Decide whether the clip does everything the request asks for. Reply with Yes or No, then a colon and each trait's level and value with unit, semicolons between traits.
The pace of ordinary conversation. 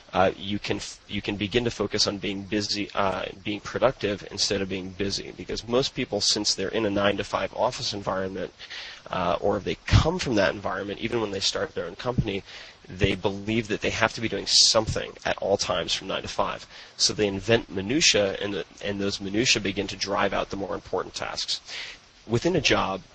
No: fast, 210 wpm